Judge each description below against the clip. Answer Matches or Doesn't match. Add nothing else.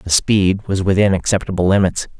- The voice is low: Matches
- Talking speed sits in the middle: Matches